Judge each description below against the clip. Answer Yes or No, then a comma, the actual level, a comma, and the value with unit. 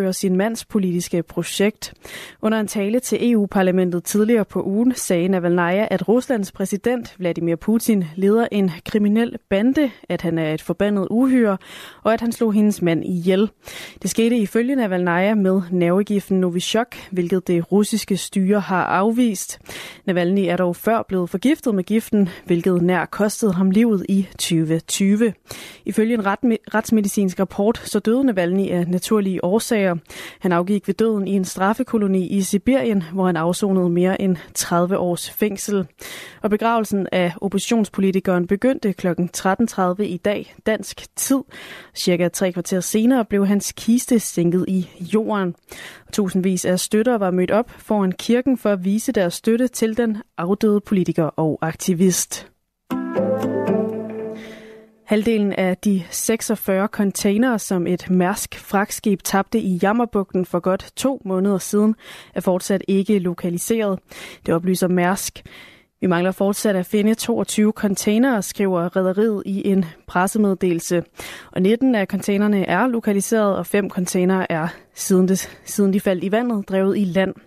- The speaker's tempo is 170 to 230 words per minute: No, slow, 145 wpm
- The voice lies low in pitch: No, high, 195 Hz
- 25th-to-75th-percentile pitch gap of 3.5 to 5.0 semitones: No, average, 3.0 semitones